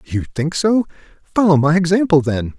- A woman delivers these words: No, male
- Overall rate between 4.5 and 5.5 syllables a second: Yes, 5.3 syllables/s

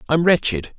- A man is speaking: Yes, male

